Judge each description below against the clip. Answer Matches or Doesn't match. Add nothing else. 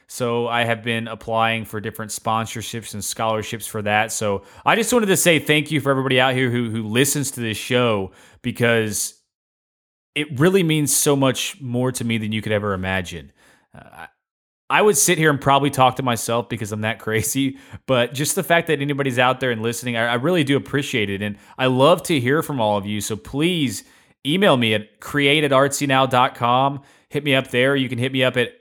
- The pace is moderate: Doesn't match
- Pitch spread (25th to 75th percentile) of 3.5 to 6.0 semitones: Matches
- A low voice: Matches